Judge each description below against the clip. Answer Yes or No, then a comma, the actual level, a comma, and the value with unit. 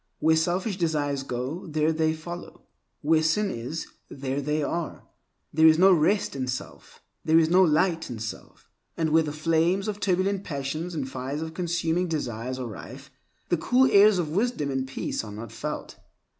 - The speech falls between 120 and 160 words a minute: No, average, 180 wpm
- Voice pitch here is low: No, medium, 160 Hz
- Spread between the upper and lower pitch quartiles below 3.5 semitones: No, average, 4.0 semitones